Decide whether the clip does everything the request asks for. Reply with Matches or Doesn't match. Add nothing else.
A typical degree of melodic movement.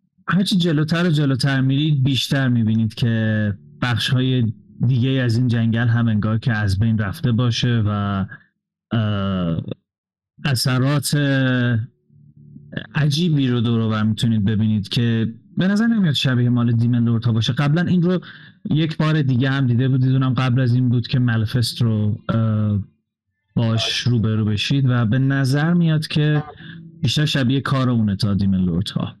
Matches